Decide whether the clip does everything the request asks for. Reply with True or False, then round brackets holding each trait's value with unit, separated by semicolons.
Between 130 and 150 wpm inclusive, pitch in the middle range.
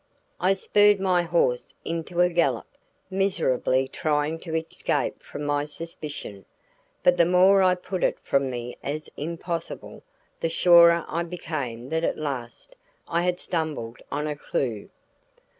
True (140 wpm; 165 Hz)